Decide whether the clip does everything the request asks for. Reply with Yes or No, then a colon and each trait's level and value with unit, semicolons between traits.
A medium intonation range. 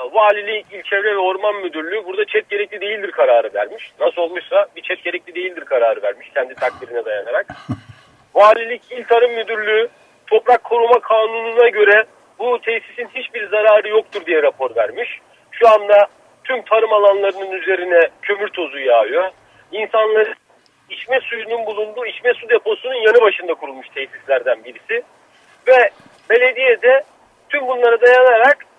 No: wide, 6.4 semitones